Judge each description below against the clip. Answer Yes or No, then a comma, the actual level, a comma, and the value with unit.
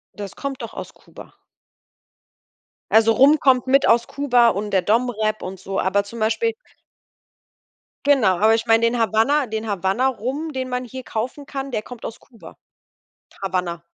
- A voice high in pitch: Yes, high, 230 Hz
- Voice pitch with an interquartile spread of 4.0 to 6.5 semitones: No, average, 3.6 semitones